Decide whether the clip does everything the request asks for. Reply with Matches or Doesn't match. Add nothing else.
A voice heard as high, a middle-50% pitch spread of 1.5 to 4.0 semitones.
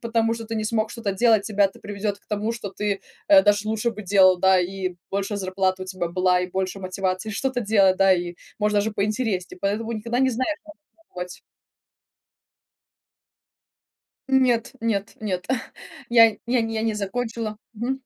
Matches